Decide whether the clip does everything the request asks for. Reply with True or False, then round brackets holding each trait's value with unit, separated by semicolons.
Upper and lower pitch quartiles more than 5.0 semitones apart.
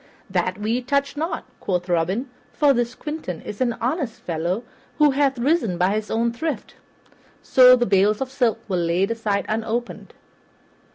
True (5.6 semitones)